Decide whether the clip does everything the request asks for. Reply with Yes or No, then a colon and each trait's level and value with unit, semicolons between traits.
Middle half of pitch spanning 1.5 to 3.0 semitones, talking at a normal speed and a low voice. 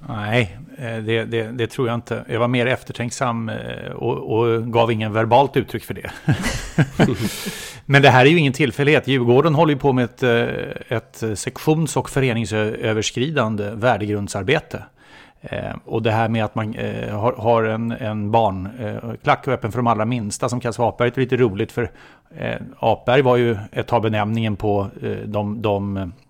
Yes: narrow, 2.5 semitones; average, 155 wpm; low, 115 Hz